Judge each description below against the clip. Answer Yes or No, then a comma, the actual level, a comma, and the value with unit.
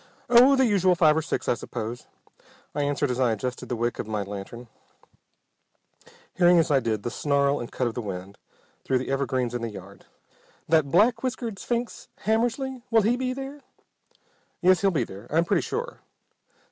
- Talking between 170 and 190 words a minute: Yes, average, 185 wpm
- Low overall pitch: No, medium, 145 Hz